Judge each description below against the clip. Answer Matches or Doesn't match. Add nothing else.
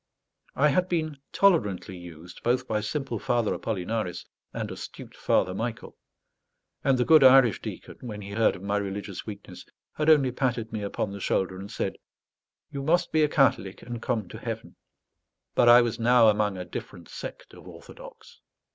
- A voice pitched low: Matches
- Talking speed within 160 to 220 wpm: Matches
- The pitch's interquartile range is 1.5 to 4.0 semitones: Doesn't match